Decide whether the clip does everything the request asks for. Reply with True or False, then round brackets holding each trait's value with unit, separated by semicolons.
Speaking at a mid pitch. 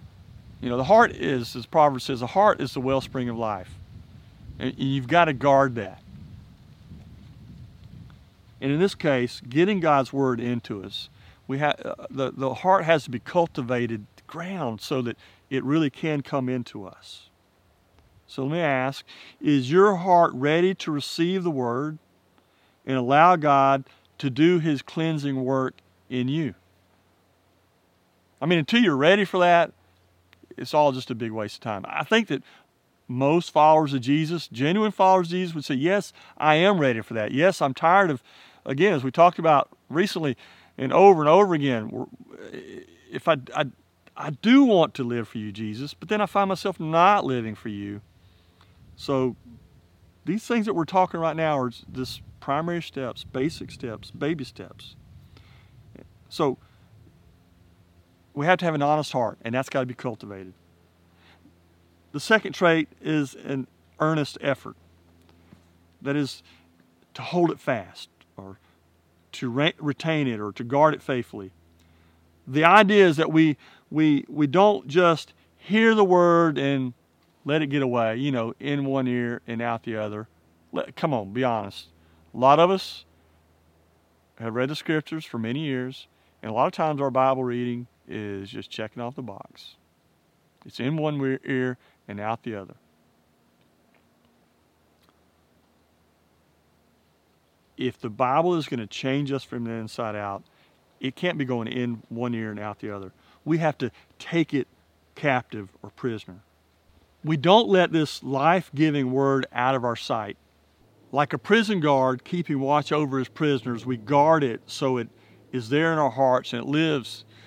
False (130 Hz)